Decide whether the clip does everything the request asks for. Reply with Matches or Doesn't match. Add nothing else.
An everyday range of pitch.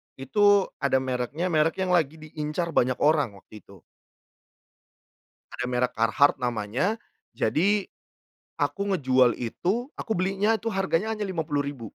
Doesn't match